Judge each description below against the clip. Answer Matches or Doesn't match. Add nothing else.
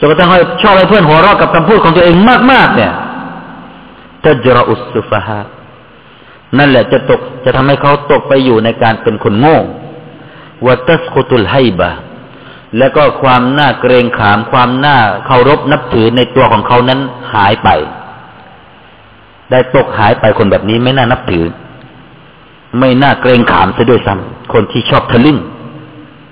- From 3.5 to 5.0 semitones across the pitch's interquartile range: Matches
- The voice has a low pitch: Matches